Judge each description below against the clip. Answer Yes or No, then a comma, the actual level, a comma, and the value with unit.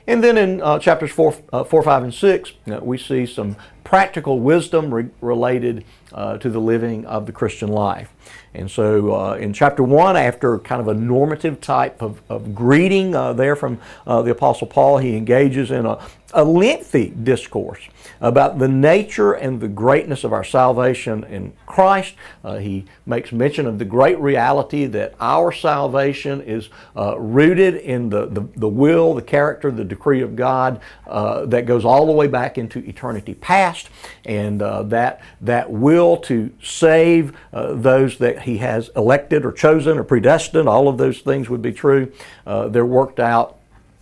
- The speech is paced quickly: No, average, 175 wpm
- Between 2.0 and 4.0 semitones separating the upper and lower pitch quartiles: No, average, 4.5 semitones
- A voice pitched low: Yes, low, 125 Hz